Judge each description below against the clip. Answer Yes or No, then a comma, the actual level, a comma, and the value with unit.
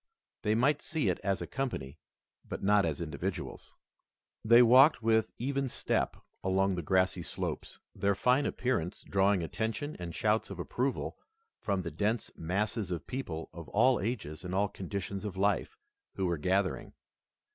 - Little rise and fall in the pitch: No, average, 4.5 semitones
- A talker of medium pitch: No, low, 100 Hz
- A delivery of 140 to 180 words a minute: Yes, average, 155 wpm